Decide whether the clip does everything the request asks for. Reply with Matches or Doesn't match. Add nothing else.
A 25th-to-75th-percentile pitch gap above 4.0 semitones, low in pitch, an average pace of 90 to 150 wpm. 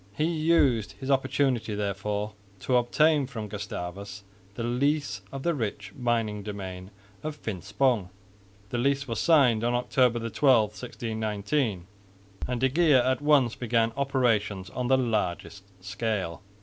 Matches